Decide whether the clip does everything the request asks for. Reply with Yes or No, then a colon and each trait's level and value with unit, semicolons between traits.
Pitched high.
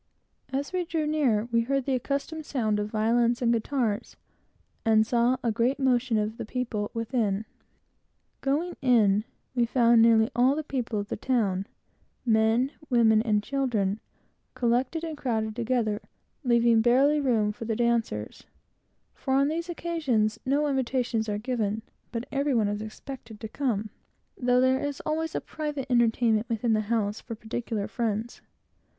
Yes: high, 235 Hz